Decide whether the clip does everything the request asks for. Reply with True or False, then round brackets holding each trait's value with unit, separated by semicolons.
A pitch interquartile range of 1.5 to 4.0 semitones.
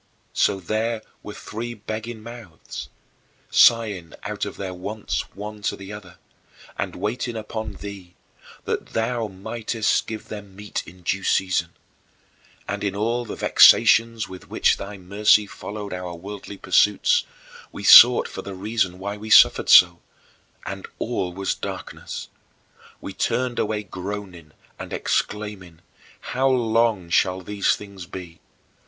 True (2.8 semitones)